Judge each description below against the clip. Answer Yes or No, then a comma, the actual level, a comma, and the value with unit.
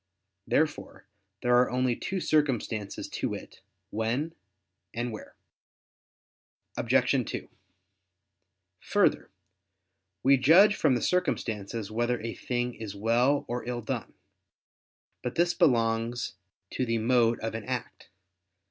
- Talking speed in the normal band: No, slow, 115 wpm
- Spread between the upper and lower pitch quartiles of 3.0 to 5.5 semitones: No, narrow, 2.6 semitones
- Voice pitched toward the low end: Yes, low, 120 Hz